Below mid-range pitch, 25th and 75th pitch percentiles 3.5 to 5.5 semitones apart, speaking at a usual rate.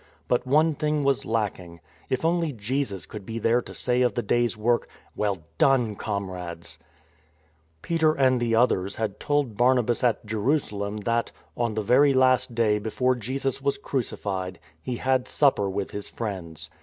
Yes: low, 115 Hz; average, 4.3 semitones; average, 175 wpm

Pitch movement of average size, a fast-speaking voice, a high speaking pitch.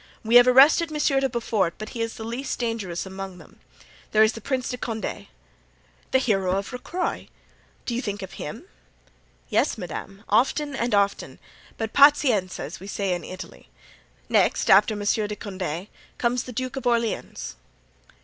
No: average, 4.2 semitones; average, 170 wpm; high, 225 Hz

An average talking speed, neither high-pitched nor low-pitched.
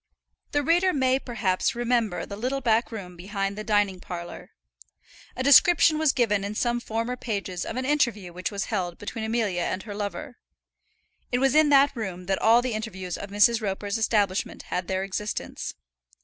No: average, 175 wpm; high, 220 Hz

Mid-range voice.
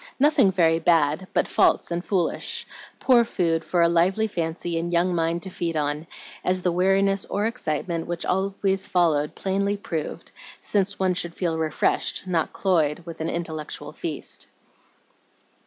Yes: medium, 175 Hz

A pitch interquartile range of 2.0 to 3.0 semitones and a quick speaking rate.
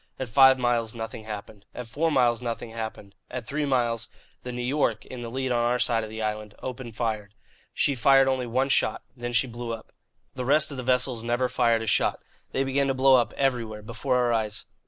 Yes: narrow, 2.5 semitones; fast, 220 wpm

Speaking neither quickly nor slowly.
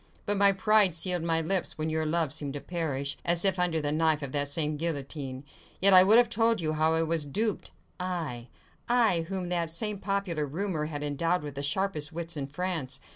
No: fast, 210 wpm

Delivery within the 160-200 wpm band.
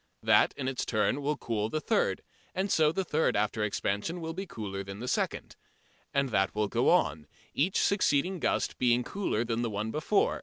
Yes: average, 195 wpm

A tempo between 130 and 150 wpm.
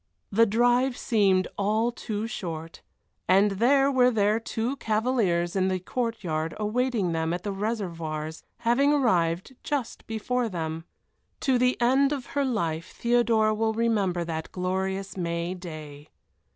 Yes: average, 140 wpm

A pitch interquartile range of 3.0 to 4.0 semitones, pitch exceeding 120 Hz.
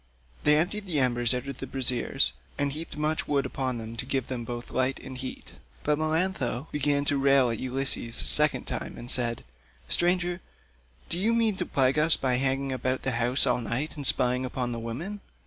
Yes: average, 3.4 semitones; low, 135 Hz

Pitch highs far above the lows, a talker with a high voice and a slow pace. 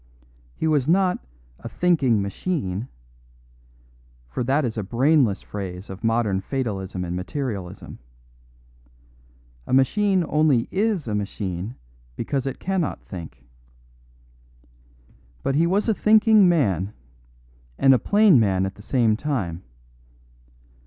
No: wide, 8.4 semitones; low, 125 Hz; slow, 120 wpm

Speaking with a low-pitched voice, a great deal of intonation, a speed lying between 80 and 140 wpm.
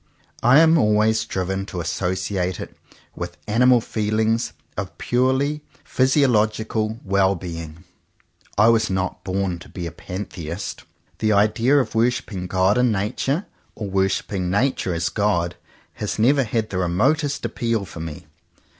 No: low, 105 Hz; average, 4.1 semitones; slow, 135 wpm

